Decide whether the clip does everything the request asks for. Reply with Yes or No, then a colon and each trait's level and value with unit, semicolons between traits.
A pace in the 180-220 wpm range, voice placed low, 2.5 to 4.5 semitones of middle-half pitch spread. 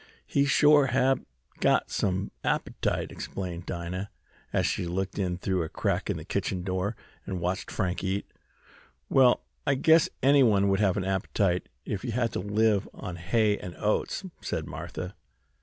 No: average, 160 wpm; low, 100 Hz; average, 4.1 semitones